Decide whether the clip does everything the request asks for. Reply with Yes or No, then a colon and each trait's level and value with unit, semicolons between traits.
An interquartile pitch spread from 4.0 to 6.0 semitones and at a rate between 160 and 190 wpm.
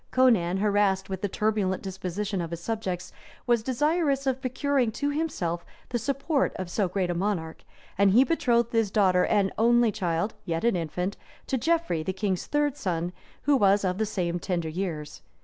Yes: average, 5.2 semitones; average, 180 wpm